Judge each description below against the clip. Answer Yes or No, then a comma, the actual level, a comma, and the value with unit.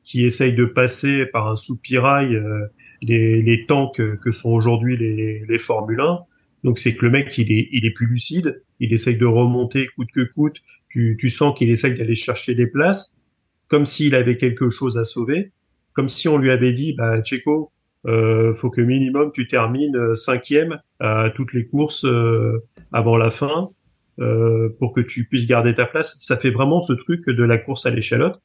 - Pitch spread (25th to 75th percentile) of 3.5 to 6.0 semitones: No, average, 2.9 semitones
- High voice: No, low, 125 Hz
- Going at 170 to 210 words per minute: Yes, average, 190 wpm